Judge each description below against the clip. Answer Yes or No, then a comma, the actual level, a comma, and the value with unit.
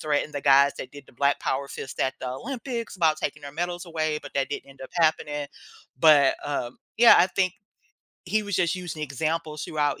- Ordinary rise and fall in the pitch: Yes, average, 3.7 semitones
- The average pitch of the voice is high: No, medium, 150 Hz